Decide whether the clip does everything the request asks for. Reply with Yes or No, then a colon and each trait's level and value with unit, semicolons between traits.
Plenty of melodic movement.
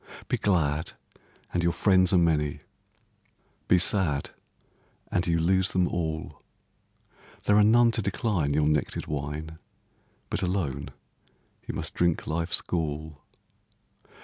No: average, 3.5 semitones